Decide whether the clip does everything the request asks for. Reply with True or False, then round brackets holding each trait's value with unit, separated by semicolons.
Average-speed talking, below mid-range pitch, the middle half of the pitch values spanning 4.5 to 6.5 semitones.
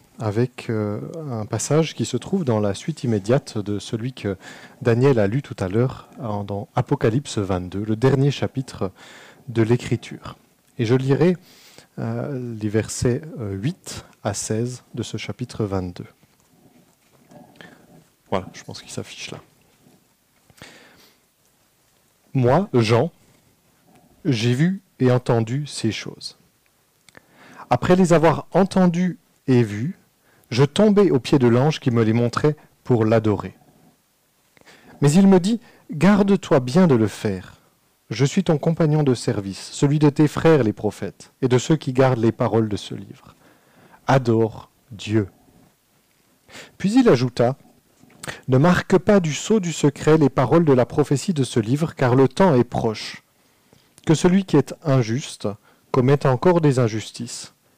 False (140 wpm; 130 Hz; 5.2 semitones)